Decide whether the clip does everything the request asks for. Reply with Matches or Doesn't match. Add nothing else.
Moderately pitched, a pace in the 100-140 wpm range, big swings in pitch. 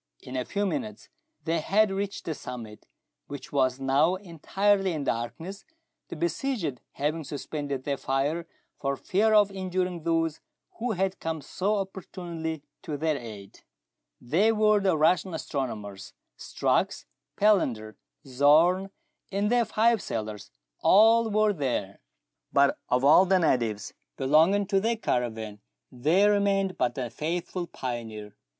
Matches